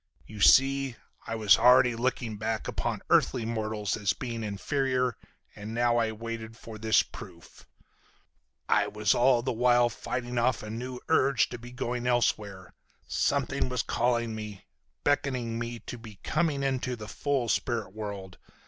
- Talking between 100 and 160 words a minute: Yes, average, 155 wpm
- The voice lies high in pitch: No, low, 120 Hz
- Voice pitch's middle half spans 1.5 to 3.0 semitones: Yes, narrow, 2.6 semitones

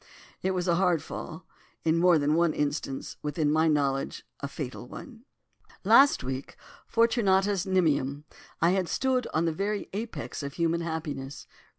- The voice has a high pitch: No, medium, 165 Hz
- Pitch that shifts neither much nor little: Yes, average, 4.5 semitones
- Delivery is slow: No, average, 155 wpm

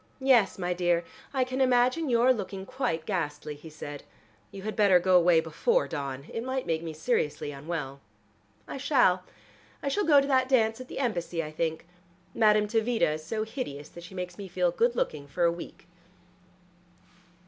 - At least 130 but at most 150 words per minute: No, average, 180 wpm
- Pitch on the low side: No, medium, 185 Hz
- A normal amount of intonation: No, wide, 7.2 semitones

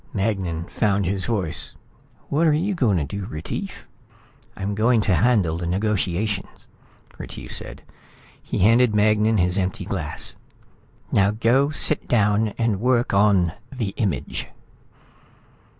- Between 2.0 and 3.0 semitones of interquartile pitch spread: No, average, 3.5 semitones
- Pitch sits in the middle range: No, low, 105 Hz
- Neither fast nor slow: No, slow, 130 wpm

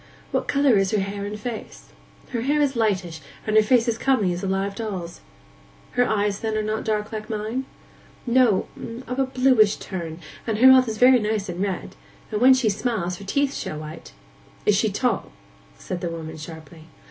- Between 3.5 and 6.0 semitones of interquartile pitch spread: Yes, average, 4.4 semitones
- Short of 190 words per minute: No, average, 195 wpm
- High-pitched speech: Yes, high, 215 Hz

